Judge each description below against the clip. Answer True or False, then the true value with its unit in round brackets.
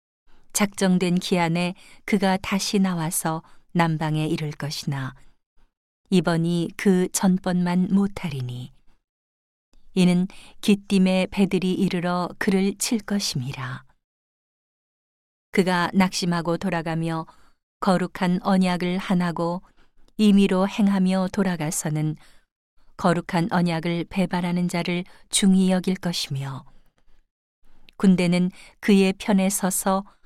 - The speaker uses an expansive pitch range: False (2.4 semitones)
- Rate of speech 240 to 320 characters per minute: False (215 characters per minute)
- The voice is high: False (180 Hz)